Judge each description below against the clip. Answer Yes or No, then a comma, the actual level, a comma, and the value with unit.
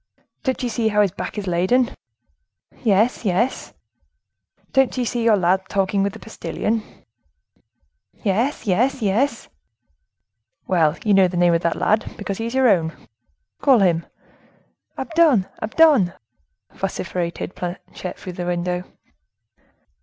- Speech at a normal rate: No, slow, 130 wpm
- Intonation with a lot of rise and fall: No, average, 4.9 semitones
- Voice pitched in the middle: No, high, 200 Hz